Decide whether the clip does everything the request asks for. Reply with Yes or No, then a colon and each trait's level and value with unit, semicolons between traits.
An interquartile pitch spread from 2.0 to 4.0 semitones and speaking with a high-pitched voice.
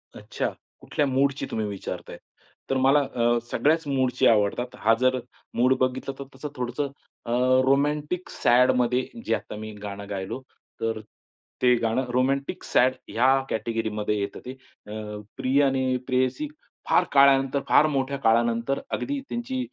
No: average, 3.2 semitones; low, 130 Hz